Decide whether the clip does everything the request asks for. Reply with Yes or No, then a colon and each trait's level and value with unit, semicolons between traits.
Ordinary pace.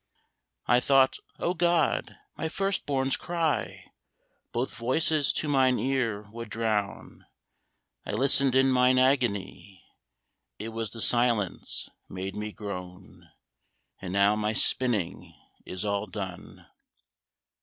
No: slow, 115 wpm